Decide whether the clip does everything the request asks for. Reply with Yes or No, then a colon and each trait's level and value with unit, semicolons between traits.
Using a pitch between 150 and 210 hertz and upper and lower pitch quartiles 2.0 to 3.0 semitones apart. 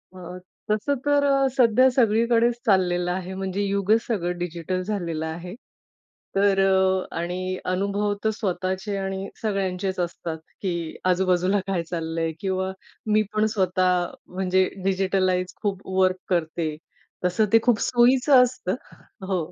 Yes: high, 190 Hz; narrow, 2.5 semitones